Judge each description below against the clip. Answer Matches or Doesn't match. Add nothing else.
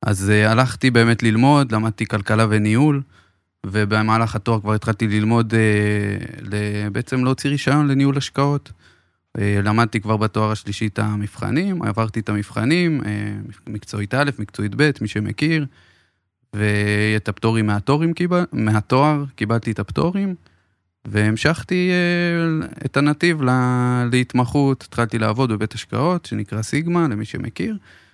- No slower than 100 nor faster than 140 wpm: Matches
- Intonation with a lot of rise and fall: Doesn't match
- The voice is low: Matches